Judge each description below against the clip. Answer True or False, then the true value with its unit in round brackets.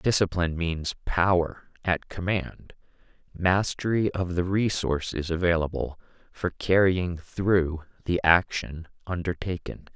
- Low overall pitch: True (90 Hz)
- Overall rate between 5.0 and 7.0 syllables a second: False (4.0 syllables/s)